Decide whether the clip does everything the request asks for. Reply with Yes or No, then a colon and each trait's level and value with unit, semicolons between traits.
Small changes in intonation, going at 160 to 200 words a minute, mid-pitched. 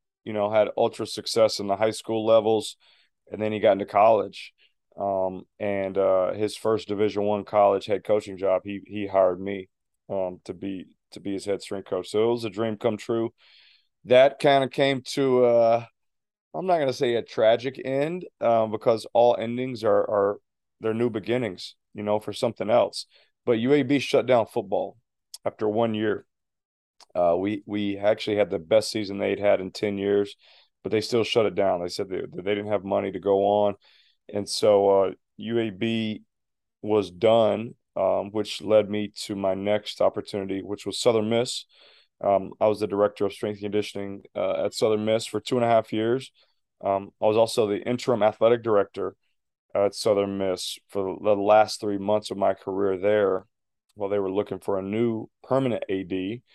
No: narrow, 2.2 semitones; average, 190 wpm; low, 105 Hz